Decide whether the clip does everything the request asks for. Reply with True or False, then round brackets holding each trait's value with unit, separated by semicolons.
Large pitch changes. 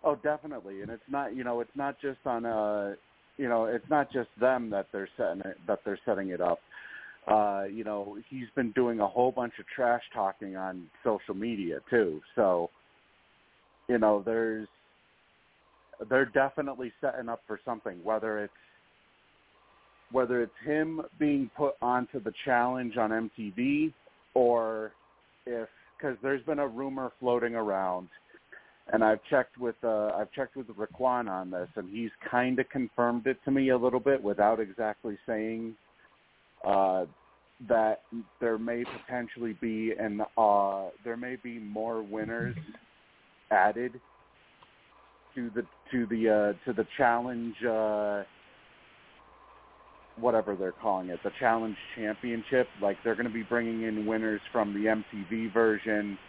False (3.0 semitones)